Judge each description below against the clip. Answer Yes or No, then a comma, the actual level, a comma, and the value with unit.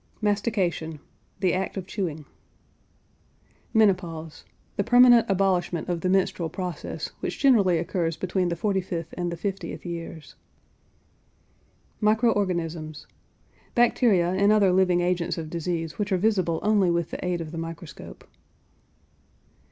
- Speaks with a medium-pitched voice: Yes, medium, 180 Hz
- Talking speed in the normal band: No, slow, 130 wpm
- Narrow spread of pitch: No, average, 3.2 semitones